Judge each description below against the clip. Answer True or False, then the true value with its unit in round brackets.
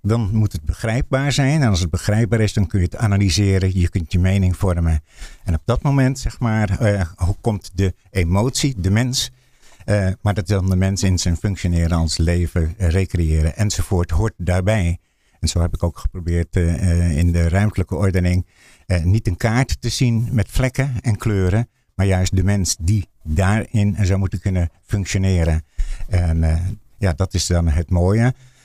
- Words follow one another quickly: False (185 wpm)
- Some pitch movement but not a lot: True (3.7 semitones)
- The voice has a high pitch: False (95 Hz)